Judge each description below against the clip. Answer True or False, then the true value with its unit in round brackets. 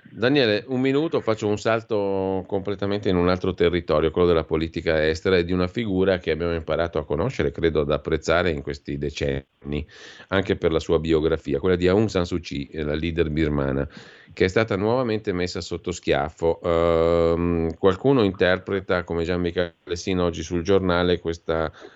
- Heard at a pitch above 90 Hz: False (85 Hz)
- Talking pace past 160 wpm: True (170 wpm)